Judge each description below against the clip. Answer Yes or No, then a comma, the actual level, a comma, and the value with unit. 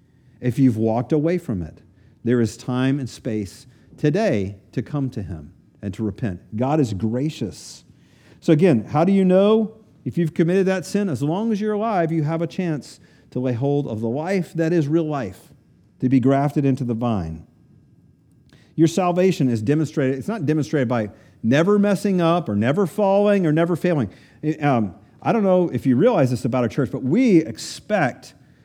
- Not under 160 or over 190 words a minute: Yes, average, 185 wpm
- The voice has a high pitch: No, medium, 140 Hz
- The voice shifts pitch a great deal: Yes, wide, 6.0 semitones